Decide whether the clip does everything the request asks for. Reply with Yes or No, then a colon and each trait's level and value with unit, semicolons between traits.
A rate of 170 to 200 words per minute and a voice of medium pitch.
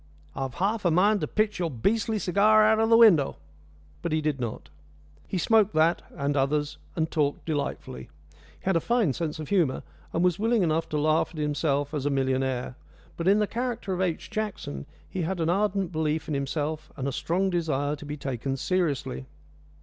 Yes: average, 195 wpm; medium, 160 Hz